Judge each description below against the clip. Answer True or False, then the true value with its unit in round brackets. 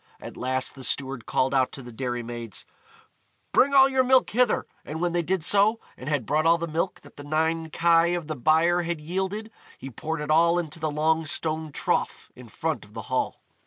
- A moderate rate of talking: False (215 wpm)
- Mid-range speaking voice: True (160 Hz)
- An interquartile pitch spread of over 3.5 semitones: True (4.2 semitones)